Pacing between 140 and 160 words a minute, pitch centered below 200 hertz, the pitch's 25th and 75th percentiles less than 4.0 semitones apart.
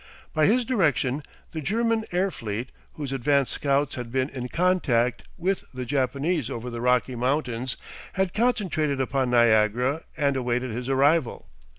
No: average, 150 wpm; low, 135 Hz; average, 4.9 semitones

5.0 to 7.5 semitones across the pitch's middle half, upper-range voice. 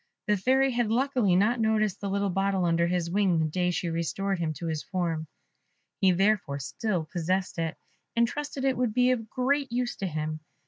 Yes: wide, 5.5 semitones; high, 195 Hz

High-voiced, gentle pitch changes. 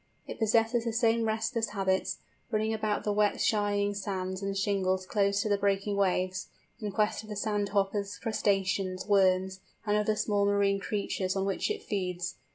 Yes: high, 200 Hz; narrow, 1.7 semitones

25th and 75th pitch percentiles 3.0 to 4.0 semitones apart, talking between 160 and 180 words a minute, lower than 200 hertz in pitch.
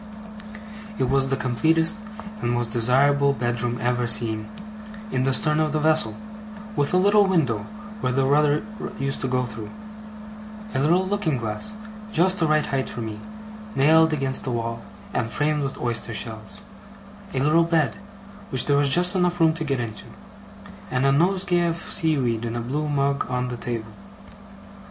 No: average, 4.8 semitones; average, 170 wpm; low, 135 Hz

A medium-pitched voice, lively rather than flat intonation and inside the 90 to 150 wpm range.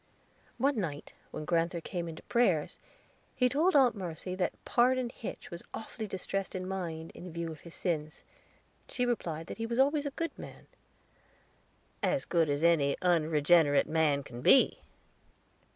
No: medium, 175 Hz; wide, 6.8 semitones; average, 160 wpm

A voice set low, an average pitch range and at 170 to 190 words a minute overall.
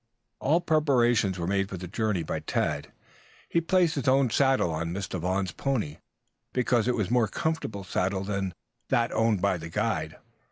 No: low, 105 Hz; wide, 5.9 semitones; average, 175 wpm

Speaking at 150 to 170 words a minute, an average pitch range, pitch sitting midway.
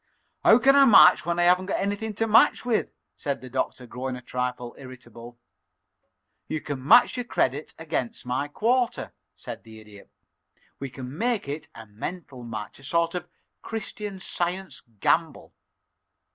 No: average, 155 wpm; wide, 8.2 semitones; medium, 150 Hz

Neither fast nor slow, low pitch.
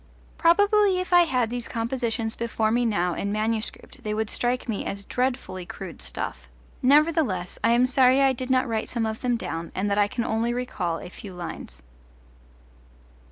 No: average, 180 wpm; high, 230 Hz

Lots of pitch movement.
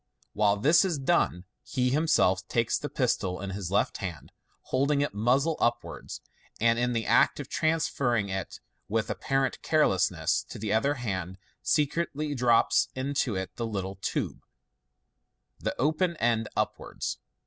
Yes: wide, 6.1 semitones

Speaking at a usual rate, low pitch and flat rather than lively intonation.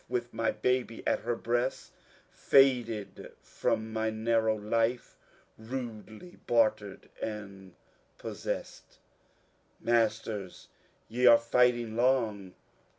No: slow, 90 wpm; low, 115 Hz; narrow, 1.9 semitones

